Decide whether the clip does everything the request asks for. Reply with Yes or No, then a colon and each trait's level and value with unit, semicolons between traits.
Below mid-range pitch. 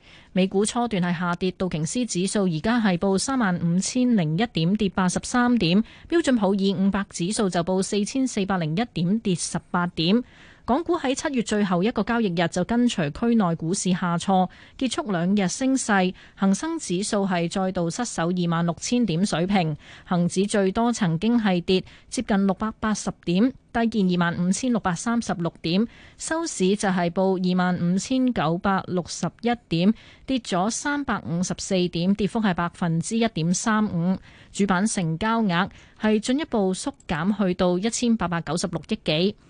No: high, 195 Hz